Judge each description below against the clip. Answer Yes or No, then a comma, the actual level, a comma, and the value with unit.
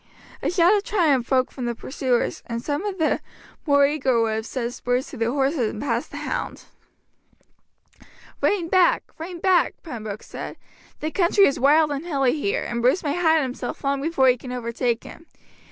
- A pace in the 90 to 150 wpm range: No, average, 185 wpm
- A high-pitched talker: Yes, very high, 275 Hz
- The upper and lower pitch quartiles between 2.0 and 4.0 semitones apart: No, average, 5.1 semitones